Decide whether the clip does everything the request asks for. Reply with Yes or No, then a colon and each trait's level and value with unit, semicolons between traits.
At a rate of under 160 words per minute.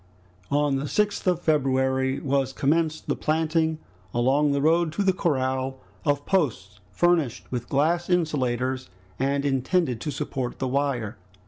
Yes: average, 140 wpm